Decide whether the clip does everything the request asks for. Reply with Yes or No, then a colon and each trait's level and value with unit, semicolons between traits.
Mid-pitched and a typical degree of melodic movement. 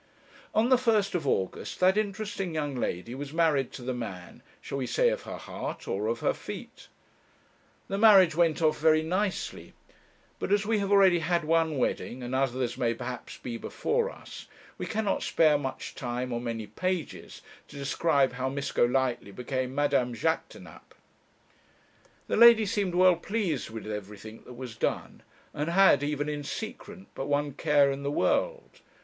No: medium, 145 Hz; wide, 6.8 semitones